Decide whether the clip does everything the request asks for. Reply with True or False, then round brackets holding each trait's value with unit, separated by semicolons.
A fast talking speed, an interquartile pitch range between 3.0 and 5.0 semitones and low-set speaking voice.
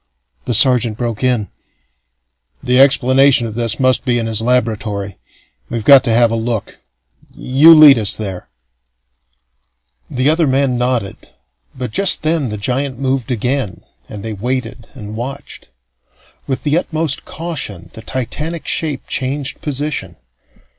False (140 wpm; 3.6 semitones; 125 Hz)